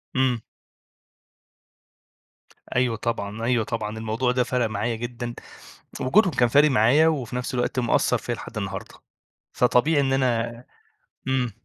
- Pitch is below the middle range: Yes, low, 120 Hz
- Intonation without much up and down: Yes, narrow, 2.1 semitones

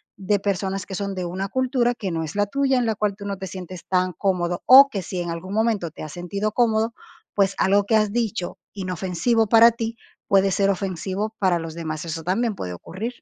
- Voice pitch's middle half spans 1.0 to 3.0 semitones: No, average, 3.4 semitones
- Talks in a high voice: Yes, high, 195 Hz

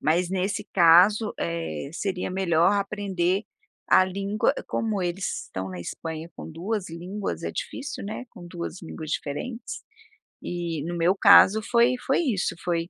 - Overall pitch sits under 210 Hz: Yes, medium, 185 Hz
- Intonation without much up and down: No, average, 3.5 semitones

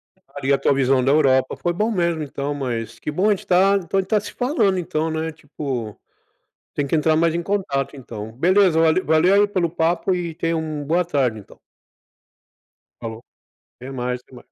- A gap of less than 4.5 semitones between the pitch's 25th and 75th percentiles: No, average, 4.8 semitones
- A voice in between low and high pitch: Yes, medium, 155 Hz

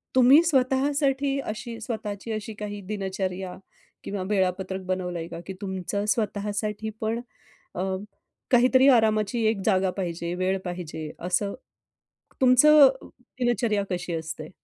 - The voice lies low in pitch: No, high, 210 Hz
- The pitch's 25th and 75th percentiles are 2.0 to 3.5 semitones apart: No, average, 4.5 semitones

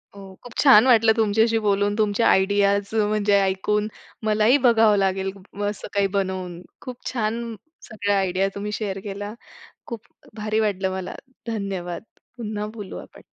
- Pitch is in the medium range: No, high, 205 Hz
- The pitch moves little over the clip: Yes, narrow, 1.9 semitones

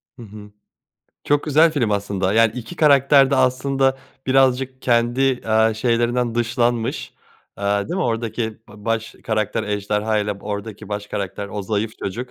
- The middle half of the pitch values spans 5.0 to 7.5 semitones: No, average, 3.8 semitones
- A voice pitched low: Yes, low, 115 Hz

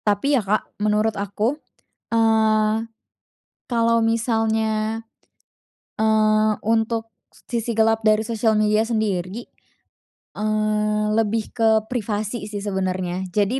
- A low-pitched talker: No, high, 215 Hz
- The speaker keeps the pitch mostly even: Yes, narrow, 1.1 semitones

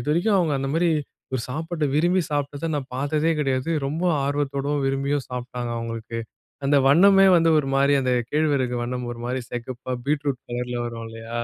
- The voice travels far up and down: No, average, 3.3 semitones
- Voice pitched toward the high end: No, medium, 140 Hz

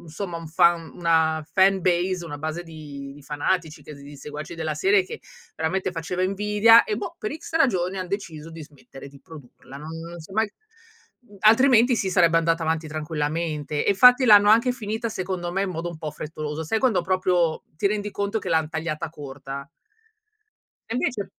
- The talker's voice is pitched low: No, medium, 170 Hz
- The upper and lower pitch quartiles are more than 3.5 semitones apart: Yes, average, 4.4 semitones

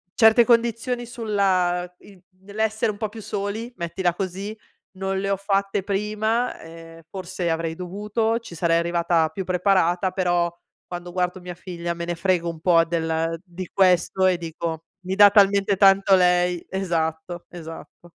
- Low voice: No, medium, 185 Hz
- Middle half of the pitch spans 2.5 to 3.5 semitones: Yes, average, 2.8 semitones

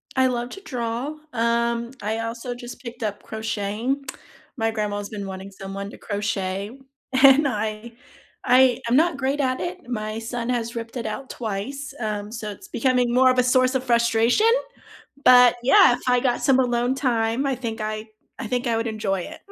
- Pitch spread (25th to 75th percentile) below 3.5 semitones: Yes, average, 2.9 semitones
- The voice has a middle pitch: No, high, 235 Hz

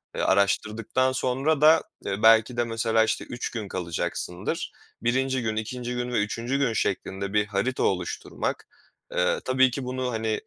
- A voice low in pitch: Yes, low, 115 Hz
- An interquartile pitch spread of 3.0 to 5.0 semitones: Yes, average, 3.6 semitones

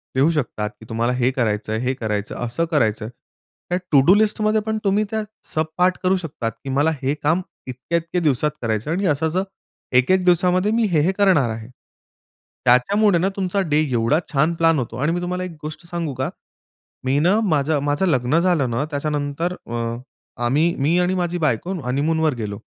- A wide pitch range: Yes, wide, 5.8 semitones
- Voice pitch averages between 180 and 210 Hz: No, medium, 155 Hz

